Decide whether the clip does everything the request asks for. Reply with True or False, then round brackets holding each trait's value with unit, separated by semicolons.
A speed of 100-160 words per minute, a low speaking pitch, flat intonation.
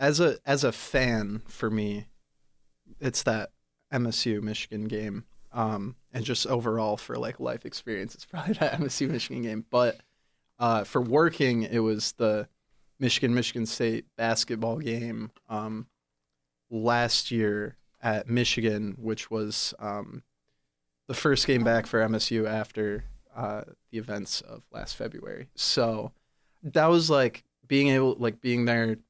True (140 wpm; 115 Hz; 2.3 semitones)